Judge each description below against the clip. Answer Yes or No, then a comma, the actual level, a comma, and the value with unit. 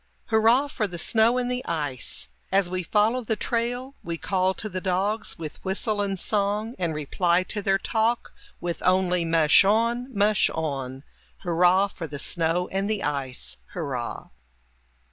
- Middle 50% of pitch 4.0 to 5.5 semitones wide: Yes, average, 4.6 semitones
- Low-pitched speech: No, high, 190 Hz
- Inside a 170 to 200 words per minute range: No, average, 160 wpm